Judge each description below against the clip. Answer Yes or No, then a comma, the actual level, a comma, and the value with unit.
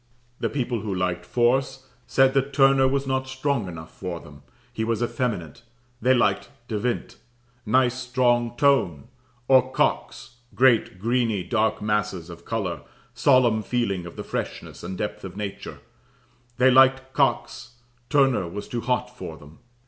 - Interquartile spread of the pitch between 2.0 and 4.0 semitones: No, average, 4.8 semitones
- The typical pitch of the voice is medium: No, low, 120 Hz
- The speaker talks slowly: No, average, 150 wpm